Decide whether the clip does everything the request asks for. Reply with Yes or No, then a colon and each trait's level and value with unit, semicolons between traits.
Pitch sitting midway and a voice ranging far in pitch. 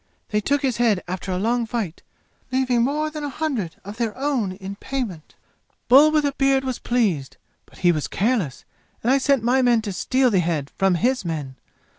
No: high, 235 Hz; wide, 5.9 semitones